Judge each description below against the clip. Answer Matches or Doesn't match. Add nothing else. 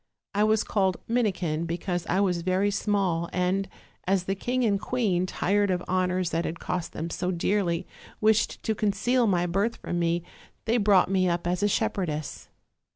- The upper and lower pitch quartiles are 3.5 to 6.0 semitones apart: Doesn't match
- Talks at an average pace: Matches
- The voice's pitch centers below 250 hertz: Matches